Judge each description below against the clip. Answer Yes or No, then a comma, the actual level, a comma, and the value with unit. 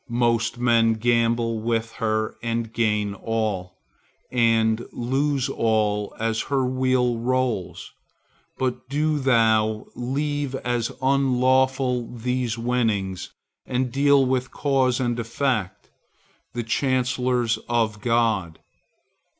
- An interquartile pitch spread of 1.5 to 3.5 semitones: Yes, narrow, 2.5 semitones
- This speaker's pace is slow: Yes, slow, 100 wpm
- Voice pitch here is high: No, low, 120 Hz